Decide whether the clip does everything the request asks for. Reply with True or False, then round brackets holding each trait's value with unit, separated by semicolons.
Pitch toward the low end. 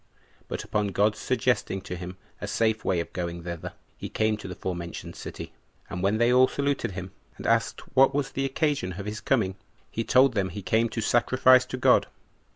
True (110 Hz)